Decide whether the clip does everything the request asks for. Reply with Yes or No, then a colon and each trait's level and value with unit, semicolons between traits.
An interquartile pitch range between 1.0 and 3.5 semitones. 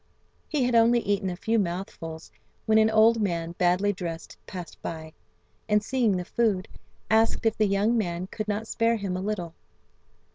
No: average, 3.9 semitones